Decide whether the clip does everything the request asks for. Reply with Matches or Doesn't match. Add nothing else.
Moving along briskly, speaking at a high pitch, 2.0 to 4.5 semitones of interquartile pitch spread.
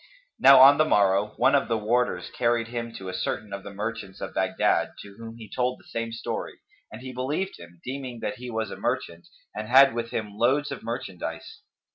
Doesn't match